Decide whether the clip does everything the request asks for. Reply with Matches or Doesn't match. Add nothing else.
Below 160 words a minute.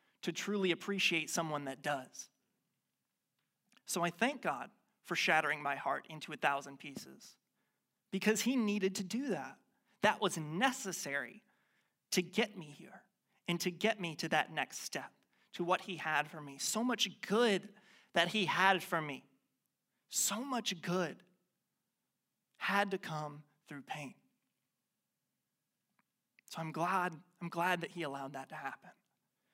Matches